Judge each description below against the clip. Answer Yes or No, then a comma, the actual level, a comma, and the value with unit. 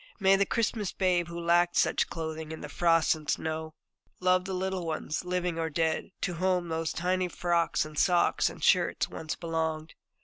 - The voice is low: No, medium, 170 Hz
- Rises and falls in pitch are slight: Yes, narrow, 2.2 semitones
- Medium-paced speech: Yes, average, 180 wpm